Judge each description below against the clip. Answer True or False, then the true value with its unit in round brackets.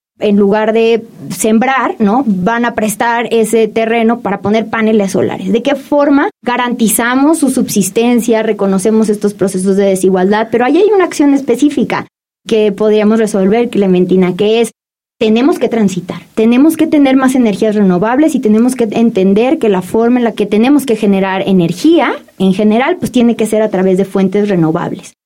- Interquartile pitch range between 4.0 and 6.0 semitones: False (3.0 semitones)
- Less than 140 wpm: False (170 wpm)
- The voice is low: False (220 Hz)